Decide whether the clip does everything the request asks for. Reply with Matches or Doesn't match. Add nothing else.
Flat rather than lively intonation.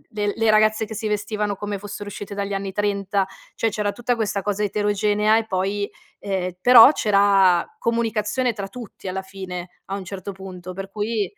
Matches